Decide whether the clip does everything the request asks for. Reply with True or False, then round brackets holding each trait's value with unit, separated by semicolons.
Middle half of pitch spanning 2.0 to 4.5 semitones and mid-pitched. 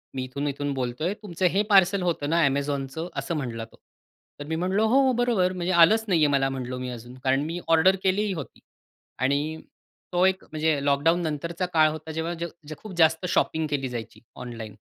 False (4.9 semitones; 160 Hz)